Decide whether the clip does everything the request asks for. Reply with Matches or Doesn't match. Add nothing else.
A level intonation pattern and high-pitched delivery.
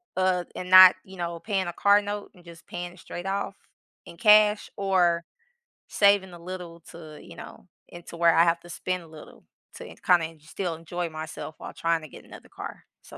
Doesn't match